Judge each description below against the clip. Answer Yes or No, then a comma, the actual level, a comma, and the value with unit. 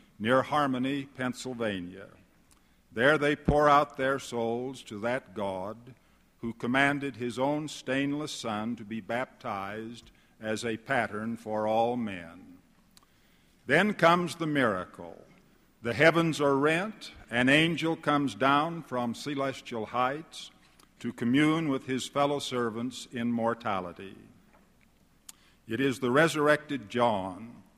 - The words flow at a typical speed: No, slow, 120 wpm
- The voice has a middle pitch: No, low, 130 Hz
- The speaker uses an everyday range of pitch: Yes, average, 4.0 semitones